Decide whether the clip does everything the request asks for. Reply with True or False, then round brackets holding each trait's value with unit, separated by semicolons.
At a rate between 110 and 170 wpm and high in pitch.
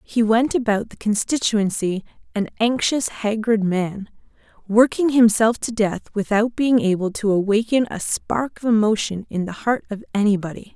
True (150 wpm; 215 Hz)